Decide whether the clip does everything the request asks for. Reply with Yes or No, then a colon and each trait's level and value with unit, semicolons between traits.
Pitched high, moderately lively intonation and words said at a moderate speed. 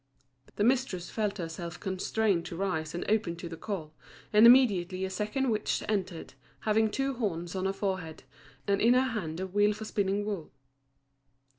Yes: high, 200 Hz; average, 3.7 semitones; average, 170 wpm